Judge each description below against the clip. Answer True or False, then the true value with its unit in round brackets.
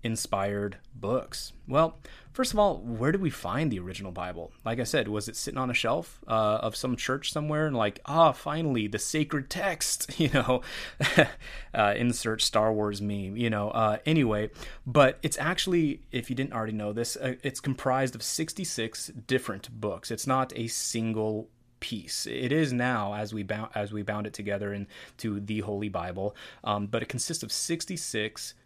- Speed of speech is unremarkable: True (185 wpm)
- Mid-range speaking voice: False (115 Hz)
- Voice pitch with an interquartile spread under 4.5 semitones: False (4.9 semitones)